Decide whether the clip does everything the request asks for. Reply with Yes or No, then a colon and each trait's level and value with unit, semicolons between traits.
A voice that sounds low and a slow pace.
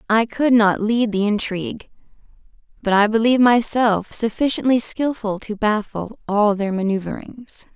No: high, 220 Hz; slow, 130 wpm